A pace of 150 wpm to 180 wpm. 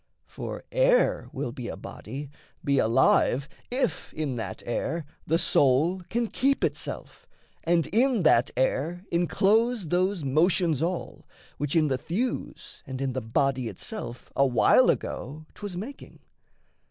No: average, 140 wpm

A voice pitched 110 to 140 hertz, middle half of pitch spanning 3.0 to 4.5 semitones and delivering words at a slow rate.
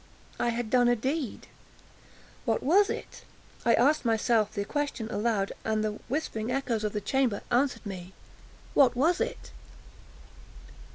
No: high, 240 Hz; average, 3.9 semitones; slow, 130 wpm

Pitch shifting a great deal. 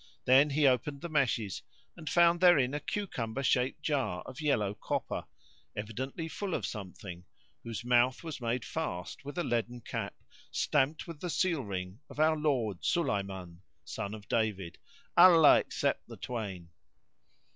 Yes: wide, 6.7 semitones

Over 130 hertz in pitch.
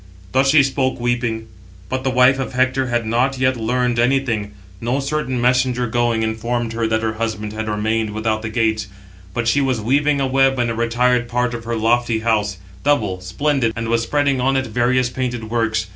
No: low, 120 Hz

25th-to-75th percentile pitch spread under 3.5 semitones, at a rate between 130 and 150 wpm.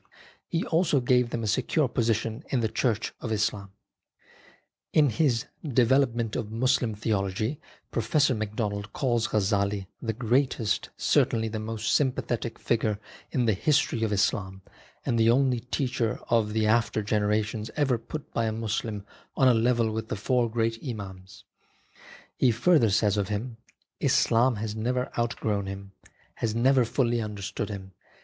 No: average, 2.7 semitones; average, 165 wpm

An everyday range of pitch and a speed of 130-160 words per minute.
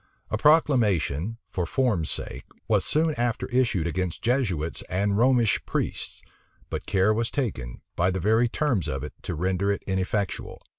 Yes: average, 5.0 semitones; average, 155 wpm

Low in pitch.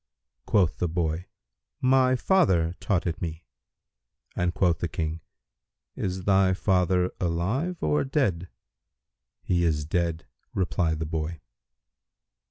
Yes: very low, 90 Hz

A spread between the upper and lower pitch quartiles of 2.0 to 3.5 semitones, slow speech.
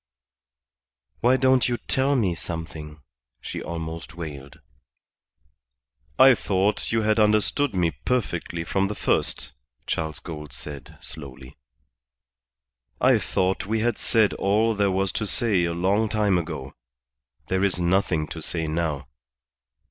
No: average, 4.9 semitones; slow, 130 wpm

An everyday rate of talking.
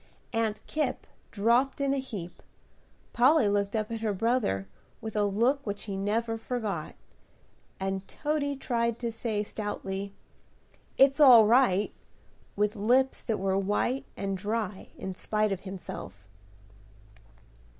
No: slow, 130 wpm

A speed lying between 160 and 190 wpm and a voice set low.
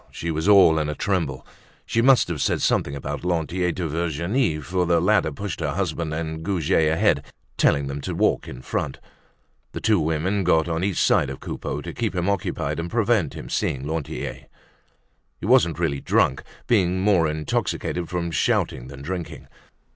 Yes: average, 180 wpm; very low, 85 Hz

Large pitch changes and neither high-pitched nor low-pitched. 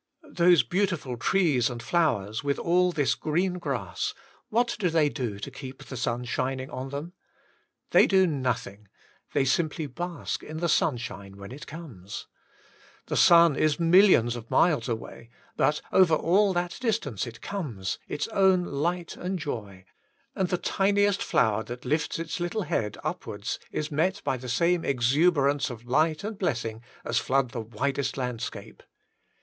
Yes: wide, 6.3 semitones; medium, 145 Hz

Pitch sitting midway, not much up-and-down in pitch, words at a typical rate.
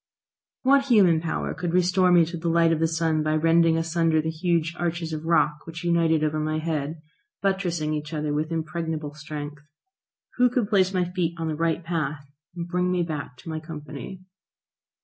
Yes: medium, 165 Hz; narrow, 2.0 semitones; average, 190 wpm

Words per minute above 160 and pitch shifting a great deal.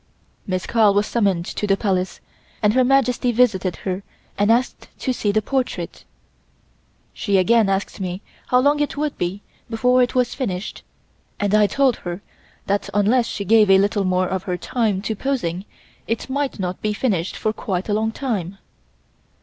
No: average, 175 wpm; average, 4.3 semitones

